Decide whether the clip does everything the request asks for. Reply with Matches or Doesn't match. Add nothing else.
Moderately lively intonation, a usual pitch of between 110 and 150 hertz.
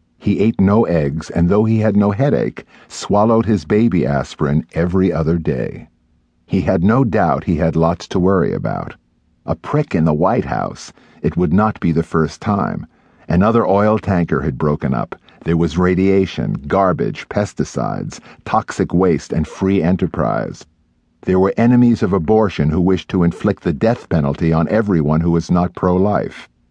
Doesn't match